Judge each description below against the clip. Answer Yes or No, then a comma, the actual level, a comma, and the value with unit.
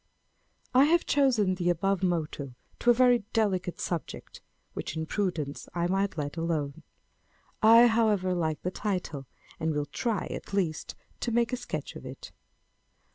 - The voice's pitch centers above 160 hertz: Yes, medium, 185 Hz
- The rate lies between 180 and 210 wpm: No, average, 155 wpm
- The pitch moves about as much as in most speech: No, wide, 5.9 semitones